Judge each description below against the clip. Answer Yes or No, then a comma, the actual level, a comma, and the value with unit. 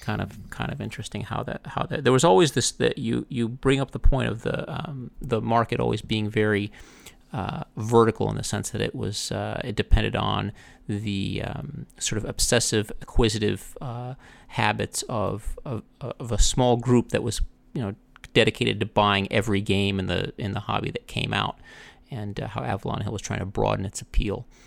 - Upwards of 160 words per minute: Yes, average, 200 wpm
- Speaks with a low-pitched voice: Yes, low, 110 Hz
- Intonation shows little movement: No, average, 3.3 semitones